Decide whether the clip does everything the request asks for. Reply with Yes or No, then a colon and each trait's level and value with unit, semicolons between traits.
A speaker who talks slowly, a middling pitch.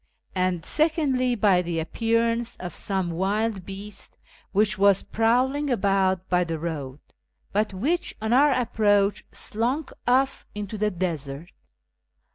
No: slow, 125 wpm; high, 205 Hz